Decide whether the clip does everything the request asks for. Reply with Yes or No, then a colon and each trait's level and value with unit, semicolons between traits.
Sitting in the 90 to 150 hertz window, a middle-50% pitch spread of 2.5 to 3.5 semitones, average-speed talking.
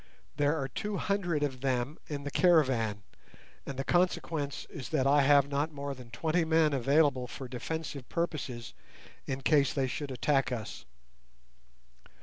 Yes: medium, 140 Hz; average, 3.1 semitones; average, 150 wpm